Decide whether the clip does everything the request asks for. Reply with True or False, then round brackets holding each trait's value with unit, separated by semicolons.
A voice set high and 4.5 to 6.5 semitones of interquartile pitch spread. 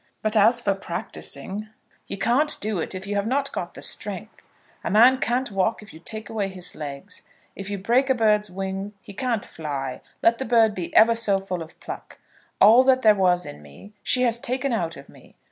False (210 Hz; 3.8 semitones)